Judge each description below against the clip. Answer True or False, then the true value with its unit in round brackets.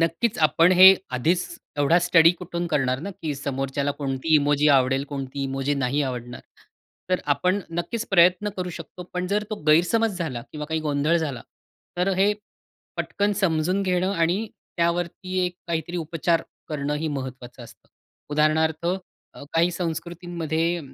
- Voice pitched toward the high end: False (165 Hz)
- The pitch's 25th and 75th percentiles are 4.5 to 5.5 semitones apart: False (3.8 semitones)